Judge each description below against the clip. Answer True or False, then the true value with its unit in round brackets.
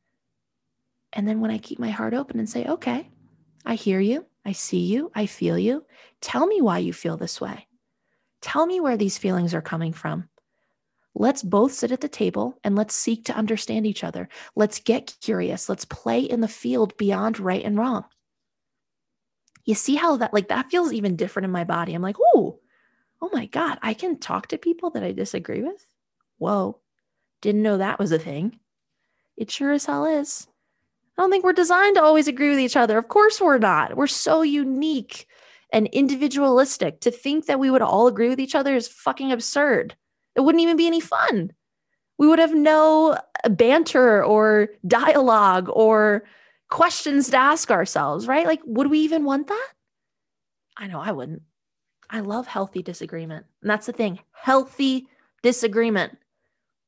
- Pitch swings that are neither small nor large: False (5.7 semitones)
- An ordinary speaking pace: True (180 wpm)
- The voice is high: True (245 Hz)